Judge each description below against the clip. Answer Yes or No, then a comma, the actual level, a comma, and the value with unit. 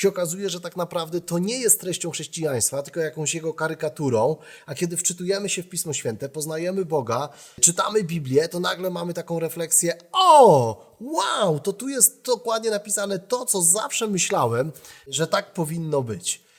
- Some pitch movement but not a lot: Yes, average, 3.8 semitones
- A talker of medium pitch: Yes, medium, 175 Hz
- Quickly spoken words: Yes, fast, 165 wpm